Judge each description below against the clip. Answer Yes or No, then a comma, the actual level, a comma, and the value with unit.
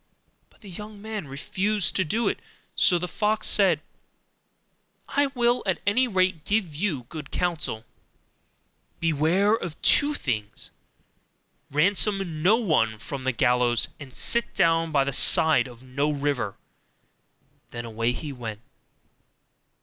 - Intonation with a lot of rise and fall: Yes, wide, 7.5 semitones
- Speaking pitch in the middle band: Yes, medium, 160 Hz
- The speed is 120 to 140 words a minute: Yes, slow, 135 wpm